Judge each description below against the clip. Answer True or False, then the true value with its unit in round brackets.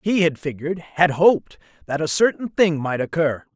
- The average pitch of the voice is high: False (160 Hz)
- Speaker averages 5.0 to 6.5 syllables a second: True (5.1 syllables/s)